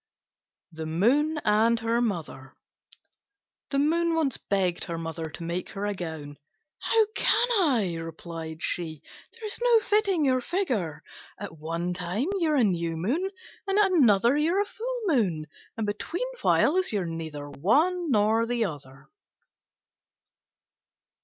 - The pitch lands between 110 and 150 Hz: No, high, 210 Hz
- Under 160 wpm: Yes, average, 140 wpm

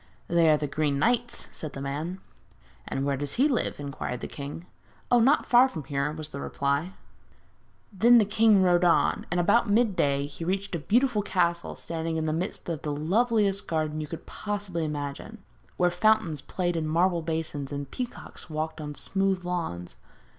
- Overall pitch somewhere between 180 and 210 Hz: No, medium, 170 Hz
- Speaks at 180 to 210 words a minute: Yes, average, 185 wpm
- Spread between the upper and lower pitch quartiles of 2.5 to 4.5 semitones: No, average, 5.1 semitones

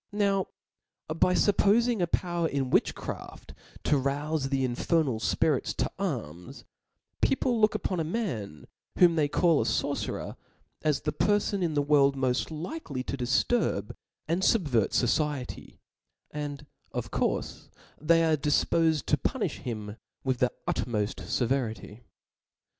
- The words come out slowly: Yes, slow, 130 wpm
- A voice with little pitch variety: No, average, 5.2 semitones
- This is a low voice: No, medium, 150 Hz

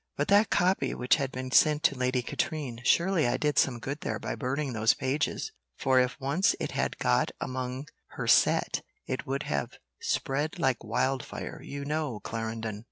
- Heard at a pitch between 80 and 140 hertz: Yes, low, 135 Hz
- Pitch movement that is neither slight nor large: Yes, average, 3.0 semitones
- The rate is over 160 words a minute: Yes, average, 175 wpm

